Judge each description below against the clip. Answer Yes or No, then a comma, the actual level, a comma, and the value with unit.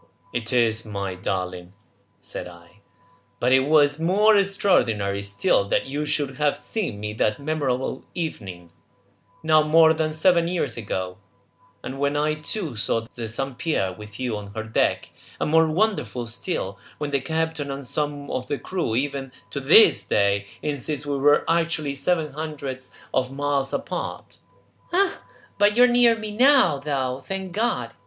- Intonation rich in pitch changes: Yes, wide, 6.2 semitones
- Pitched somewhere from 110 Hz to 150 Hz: Yes, medium, 140 Hz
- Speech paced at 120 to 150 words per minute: No, average, 160 wpm